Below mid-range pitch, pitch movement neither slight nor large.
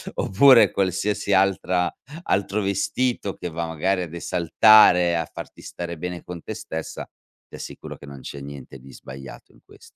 Yes: very low, 90 Hz; average, 3.3 semitones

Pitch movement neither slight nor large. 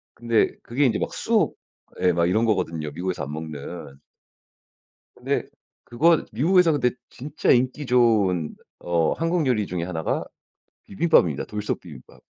No: wide, 7.1 semitones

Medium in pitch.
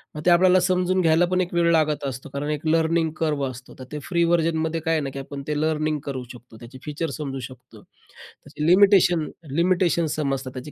Yes: medium, 155 Hz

